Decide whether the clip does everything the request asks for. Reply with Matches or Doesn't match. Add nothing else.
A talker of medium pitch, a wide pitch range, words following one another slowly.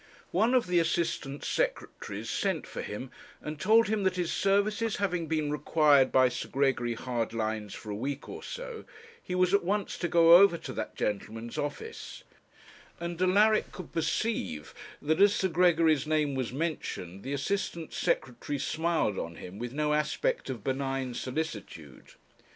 Doesn't match